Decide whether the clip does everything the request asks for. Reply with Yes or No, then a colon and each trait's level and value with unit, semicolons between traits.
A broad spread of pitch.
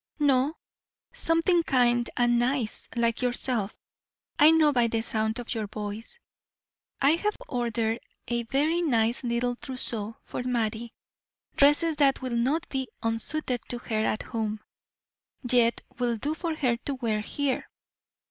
No: average, 3.8 semitones